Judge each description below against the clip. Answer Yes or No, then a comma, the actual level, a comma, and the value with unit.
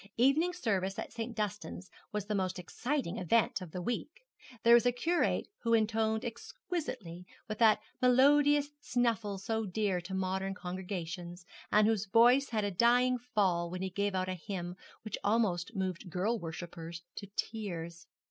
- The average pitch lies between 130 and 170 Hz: No, high, 210 Hz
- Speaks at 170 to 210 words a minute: No, average, 160 wpm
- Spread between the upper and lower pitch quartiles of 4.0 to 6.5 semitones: Yes, average, 4.5 semitones